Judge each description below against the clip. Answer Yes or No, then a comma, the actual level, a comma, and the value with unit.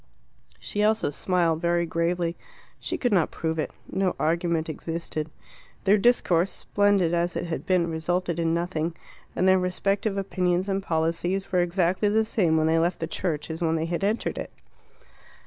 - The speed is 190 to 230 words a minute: No, average, 170 wpm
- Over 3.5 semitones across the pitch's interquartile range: No, average, 2.7 semitones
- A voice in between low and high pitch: Yes, medium, 175 Hz